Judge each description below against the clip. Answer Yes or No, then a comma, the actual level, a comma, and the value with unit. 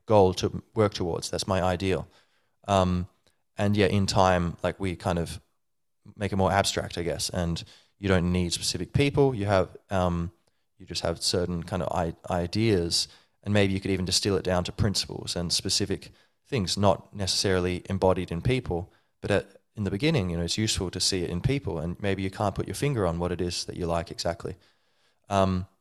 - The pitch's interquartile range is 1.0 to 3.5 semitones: Yes, narrow, 2.5 semitones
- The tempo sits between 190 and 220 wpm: Yes, average, 200 wpm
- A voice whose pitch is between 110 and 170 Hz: No, very low, 95 Hz